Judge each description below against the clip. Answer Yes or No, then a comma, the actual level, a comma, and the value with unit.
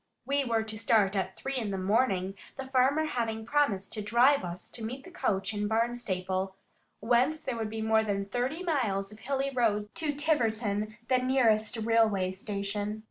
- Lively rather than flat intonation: No, average, 4.1 semitones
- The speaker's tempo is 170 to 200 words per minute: Yes, average, 180 wpm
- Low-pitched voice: No, high, 220 Hz